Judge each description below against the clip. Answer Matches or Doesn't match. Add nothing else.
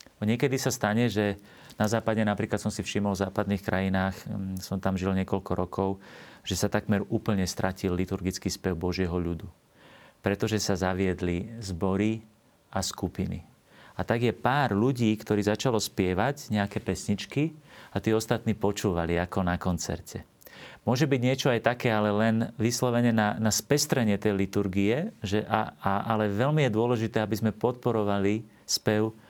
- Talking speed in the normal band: Matches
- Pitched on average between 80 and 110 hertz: Matches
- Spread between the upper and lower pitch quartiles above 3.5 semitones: Doesn't match